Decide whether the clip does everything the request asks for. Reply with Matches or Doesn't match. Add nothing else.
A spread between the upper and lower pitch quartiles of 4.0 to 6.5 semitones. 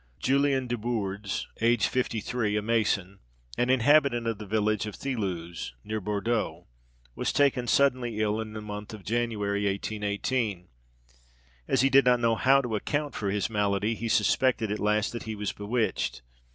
Doesn't match